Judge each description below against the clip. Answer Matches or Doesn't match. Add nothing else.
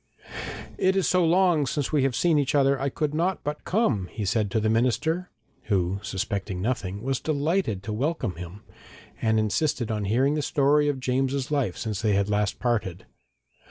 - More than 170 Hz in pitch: Doesn't match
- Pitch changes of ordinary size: Doesn't match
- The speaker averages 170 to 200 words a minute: Matches